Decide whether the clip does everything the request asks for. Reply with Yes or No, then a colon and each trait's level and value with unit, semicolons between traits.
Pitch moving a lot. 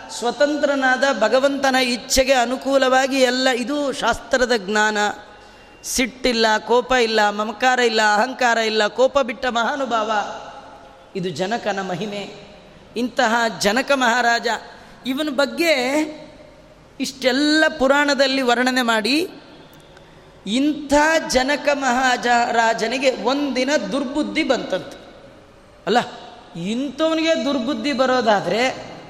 No: average, 3.4 semitones